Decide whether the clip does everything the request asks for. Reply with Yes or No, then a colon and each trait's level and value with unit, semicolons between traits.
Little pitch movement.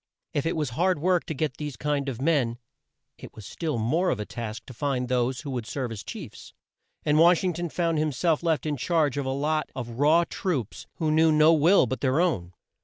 No: average, 4.3 semitones